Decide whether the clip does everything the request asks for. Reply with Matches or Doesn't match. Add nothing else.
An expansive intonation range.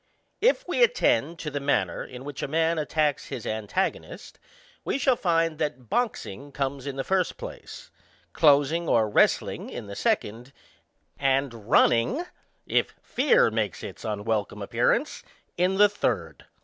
Matches